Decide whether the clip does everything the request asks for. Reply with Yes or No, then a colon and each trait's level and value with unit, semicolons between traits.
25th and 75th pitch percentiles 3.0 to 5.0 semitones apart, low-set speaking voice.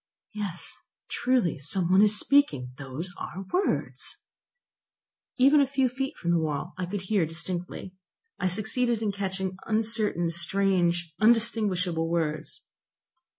No: average, 4.4 semitones; high, 190 Hz